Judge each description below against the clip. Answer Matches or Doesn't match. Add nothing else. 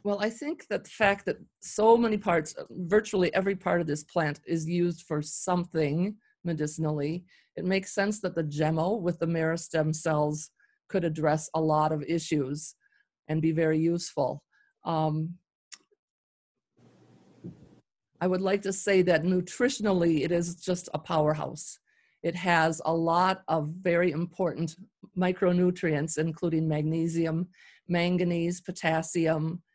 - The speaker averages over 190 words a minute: Doesn't match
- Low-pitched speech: Doesn't match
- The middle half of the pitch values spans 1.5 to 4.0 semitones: Matches